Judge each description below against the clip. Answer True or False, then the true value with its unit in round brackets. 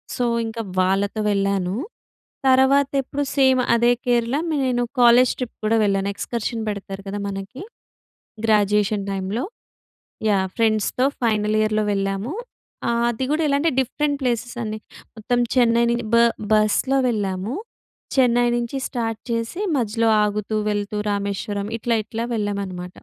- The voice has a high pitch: True (220 Hz)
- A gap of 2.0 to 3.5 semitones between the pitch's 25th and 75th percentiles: True (3.2 semitones)